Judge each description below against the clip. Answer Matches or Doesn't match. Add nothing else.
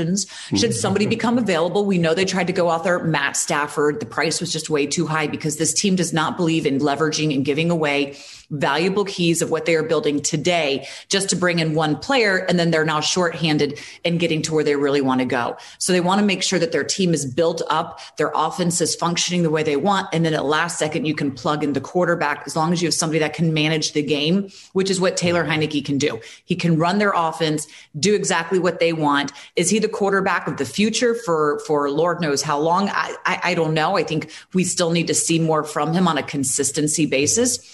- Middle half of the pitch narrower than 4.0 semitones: Matches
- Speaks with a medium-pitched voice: Matches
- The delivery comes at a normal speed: Doesn't match